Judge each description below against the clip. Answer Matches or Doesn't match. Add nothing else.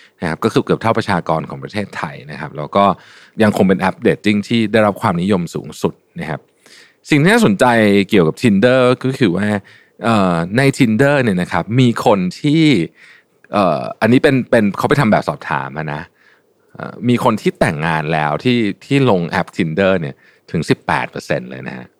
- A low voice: Matches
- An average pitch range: Doesn't match